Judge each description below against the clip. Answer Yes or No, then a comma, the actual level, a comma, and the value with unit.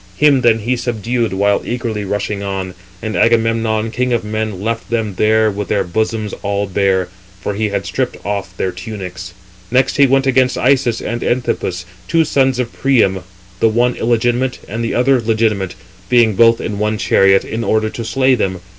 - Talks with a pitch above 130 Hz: No, low, 110 Hz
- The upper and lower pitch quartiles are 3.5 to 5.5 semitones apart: No, average, 3.1 semitones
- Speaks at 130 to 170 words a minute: No, average, 180 wpm